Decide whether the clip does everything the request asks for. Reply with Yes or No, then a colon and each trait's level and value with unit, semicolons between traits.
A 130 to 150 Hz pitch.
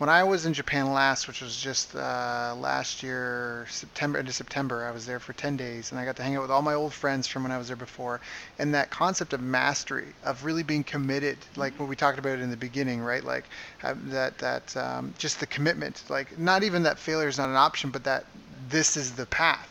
Yes: low, 135 Hz